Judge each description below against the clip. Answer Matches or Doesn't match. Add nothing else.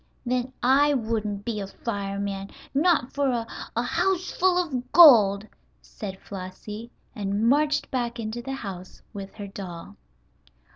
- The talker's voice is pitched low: Doesn't match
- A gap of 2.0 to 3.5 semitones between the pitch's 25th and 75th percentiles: Doesn't match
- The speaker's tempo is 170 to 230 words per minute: Doesn't match